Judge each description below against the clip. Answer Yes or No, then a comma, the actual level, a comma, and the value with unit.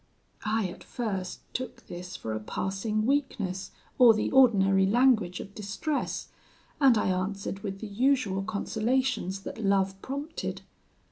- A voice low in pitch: No, high, 205 Hz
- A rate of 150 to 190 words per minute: No, slow, 135 wpm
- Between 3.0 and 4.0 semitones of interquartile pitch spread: No, average, 4.5 semitones